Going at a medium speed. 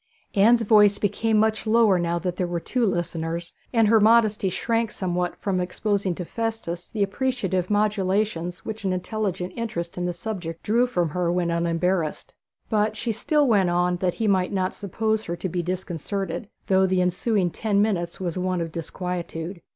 Yes: average, 175 wpm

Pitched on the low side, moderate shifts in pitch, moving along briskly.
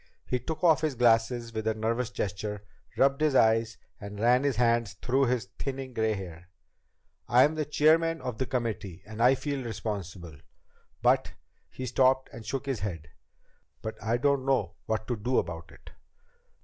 No: low, 120 Hz; average, 3.7 semitones; average, 175 wpm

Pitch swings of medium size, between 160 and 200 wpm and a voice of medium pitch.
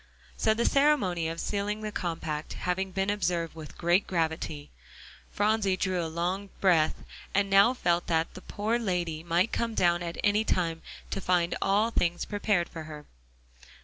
Yes: average, 3.4 semitones; average, 165 wpm; medium, 180 Hz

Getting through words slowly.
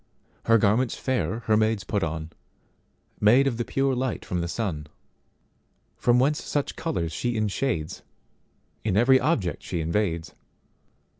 Yes: slow, 125 wpm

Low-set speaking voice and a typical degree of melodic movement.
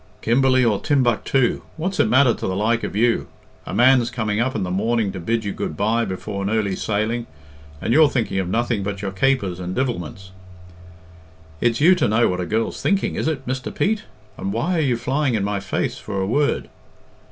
Yes: low, 115 Hz; average, 4.5 semitones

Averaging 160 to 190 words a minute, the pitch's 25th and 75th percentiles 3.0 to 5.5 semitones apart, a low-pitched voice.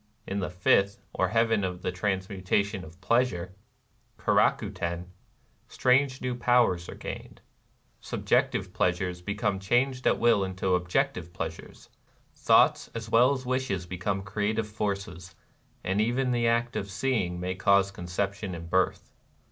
No: average, 150 wpm; average, 4.4 semitones; low, 100 Hz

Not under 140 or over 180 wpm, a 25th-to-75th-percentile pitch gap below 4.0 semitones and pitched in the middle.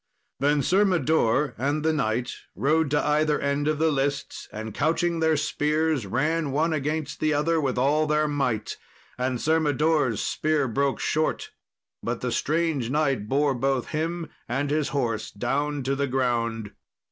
Yes: average, 160 wpm; average, 2.8 semitones; medium, 145 Hz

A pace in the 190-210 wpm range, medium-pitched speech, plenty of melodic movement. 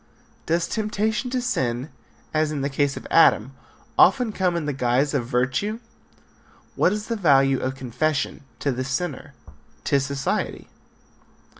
No: average, 145 wpm; medium, 145 Hz; wide, 6.2 semitones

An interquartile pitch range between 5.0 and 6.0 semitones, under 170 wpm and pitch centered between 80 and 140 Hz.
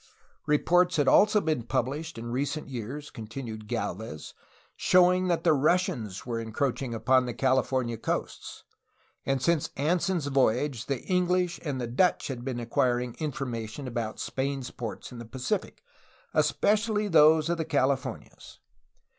Yes: average, 5.3 semitones; average, 145 wpm; low, 135 Hz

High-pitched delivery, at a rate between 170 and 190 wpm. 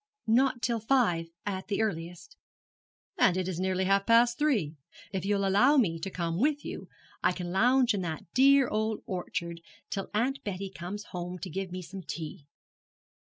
Yes: high, 195 Hz; average, 175 wpm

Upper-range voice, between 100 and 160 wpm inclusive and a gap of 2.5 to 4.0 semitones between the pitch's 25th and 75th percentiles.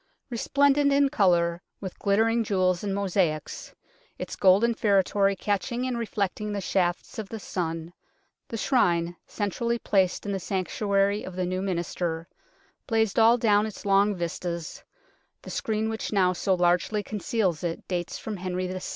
Yes: high, 195 Hz; average, 150 wpm; average, 3.4 semitones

